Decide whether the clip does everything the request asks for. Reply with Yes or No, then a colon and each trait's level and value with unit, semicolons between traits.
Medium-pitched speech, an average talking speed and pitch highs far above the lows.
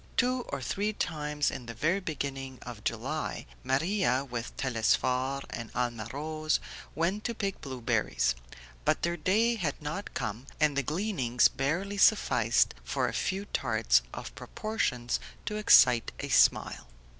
Yes: medium, 145 Hz; average, 145 wpm; wide, 7.6 semitones